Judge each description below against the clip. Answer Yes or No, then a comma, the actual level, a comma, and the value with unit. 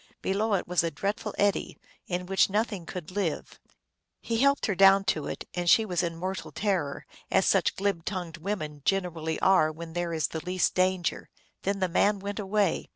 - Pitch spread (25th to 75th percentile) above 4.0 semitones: No, average, 3.1 semitones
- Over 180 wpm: Yes, average, 190 wpm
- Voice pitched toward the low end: No, medium, 185 Hz